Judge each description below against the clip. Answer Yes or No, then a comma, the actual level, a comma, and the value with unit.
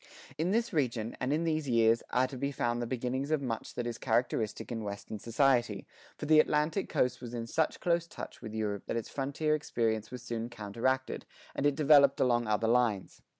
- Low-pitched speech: Yes, low, 125 Hz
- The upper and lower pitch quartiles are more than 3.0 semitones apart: Yes, average, 3.9 semitones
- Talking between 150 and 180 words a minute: No, fast, 205 wpm